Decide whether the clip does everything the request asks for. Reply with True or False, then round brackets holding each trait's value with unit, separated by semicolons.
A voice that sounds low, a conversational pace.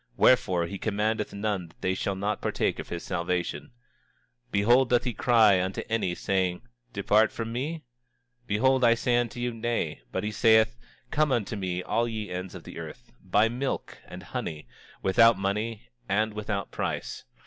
True (105 Hz; 170 wpm)